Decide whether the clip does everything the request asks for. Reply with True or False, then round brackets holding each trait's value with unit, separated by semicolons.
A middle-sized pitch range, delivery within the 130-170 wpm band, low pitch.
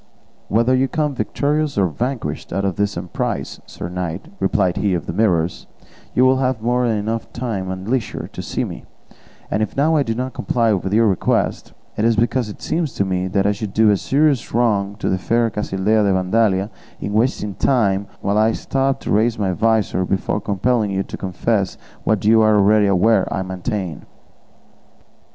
False (3.5 semitones; 190 wpm; 105 Hz)